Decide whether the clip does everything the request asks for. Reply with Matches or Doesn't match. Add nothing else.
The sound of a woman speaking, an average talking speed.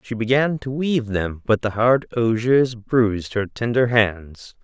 Doesn't match